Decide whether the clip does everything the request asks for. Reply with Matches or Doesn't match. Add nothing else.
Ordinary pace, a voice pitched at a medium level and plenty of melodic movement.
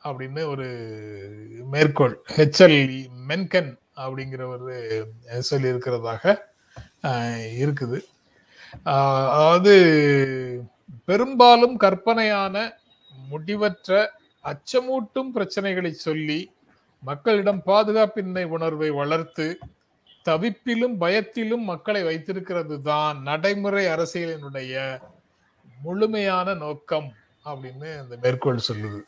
Doesn't match